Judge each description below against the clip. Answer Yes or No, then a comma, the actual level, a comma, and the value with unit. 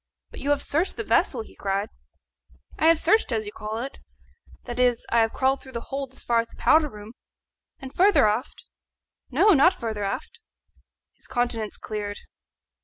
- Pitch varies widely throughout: No, average, 4.8 semitones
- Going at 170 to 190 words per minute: Yes, average, 180 wpm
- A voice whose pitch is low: No, high, 245 Hz